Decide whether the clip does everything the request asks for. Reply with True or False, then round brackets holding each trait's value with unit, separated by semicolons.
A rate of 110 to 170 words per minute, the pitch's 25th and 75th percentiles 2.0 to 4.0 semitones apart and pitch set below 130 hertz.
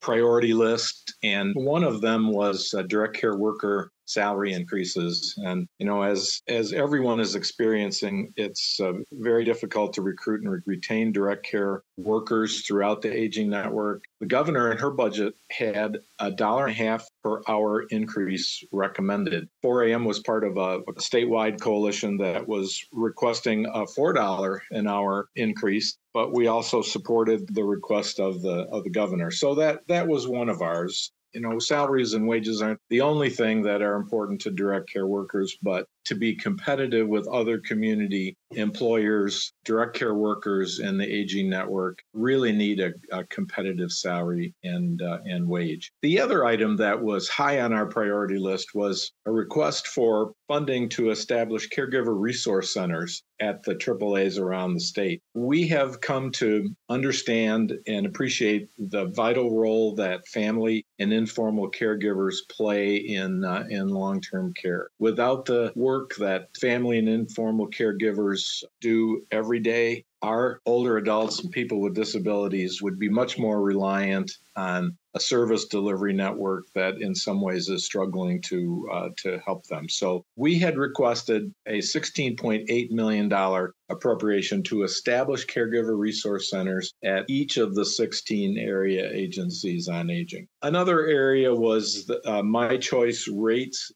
True (155 wpm; 3.0 semitones; 110 Hz)